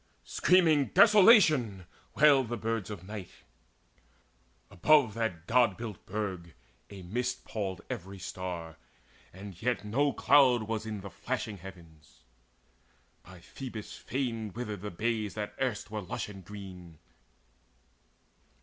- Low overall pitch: Yes, low, 105 Hz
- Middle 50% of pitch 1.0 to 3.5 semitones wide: No, average, 4.6 semitones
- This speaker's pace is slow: Yes, slow, 120 wpm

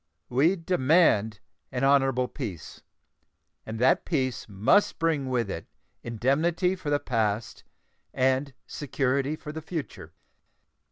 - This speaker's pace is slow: Yes, slow, 115 wpm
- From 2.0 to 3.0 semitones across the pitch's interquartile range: No, average, 4.5 semitones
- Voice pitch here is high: No, low, 135 Hz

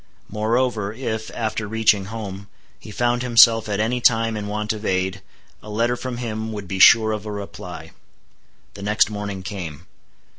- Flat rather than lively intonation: Yes, narrow, 1.9 semitones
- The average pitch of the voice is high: No, low, 110 Hz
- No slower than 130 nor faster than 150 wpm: No, average, 170 wpm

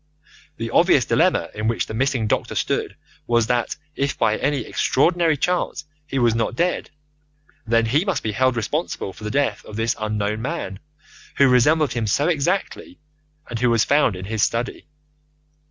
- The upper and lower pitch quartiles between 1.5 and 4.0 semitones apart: No, average, 4.5 semitones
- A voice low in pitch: Yes, low, 120 Hz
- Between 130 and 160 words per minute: No, average, 170 wpm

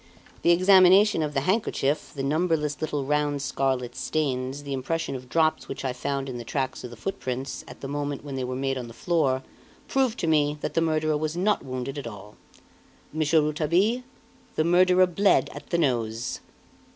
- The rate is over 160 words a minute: Yes, average, 190 wpm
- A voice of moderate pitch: Yes, medium, 145 Hz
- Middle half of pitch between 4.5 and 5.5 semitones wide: No, average, 3.8 semitones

